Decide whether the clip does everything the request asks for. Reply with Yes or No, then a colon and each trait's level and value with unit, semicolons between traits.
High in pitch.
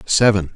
No: low, 100 Hz